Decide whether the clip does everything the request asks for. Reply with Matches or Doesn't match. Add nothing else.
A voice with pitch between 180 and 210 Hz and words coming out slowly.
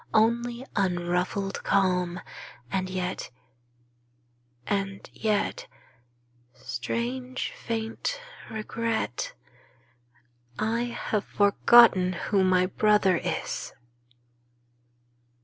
Matches